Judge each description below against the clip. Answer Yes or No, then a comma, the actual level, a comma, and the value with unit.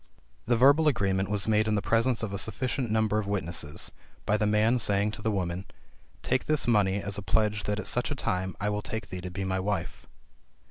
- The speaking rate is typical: No, fast, 225 wpm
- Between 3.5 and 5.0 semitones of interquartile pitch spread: No, narrow, 2.4 semitones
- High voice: No, low, 105 Hz